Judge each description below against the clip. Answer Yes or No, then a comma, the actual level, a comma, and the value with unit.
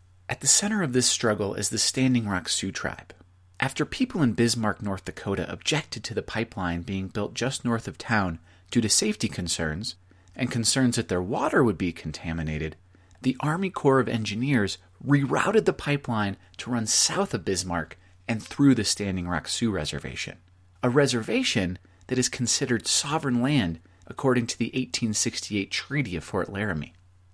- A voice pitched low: Yes, low, 105 Hz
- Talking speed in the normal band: Yes, average, 165 wpm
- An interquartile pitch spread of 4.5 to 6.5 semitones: Yes, wide, 5.6 semitones